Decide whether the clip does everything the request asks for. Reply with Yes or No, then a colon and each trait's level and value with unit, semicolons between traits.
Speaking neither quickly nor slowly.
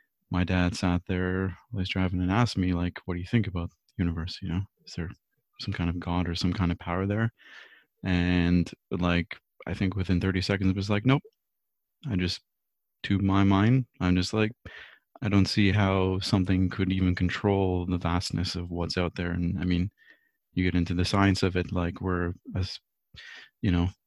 Yes: average, 195 wpm